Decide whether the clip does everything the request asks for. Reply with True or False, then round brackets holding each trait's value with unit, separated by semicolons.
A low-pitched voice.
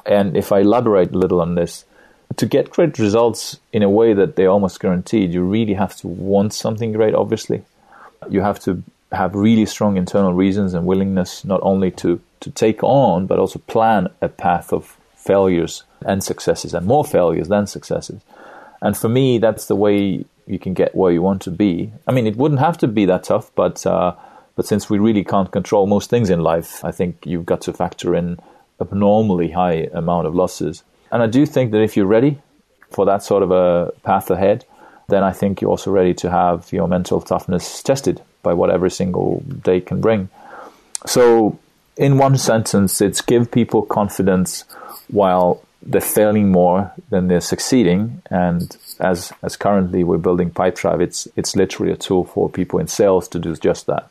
True (100 Hz)